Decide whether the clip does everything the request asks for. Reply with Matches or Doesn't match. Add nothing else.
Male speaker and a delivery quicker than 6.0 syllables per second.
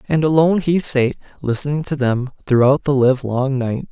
Doesn't match